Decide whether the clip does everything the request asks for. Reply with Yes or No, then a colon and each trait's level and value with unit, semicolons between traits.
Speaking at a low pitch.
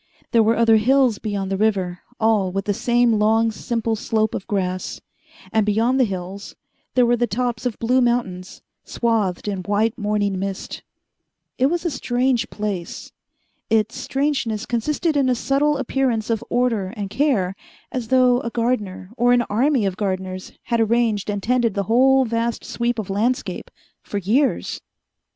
No: high, 225 Hz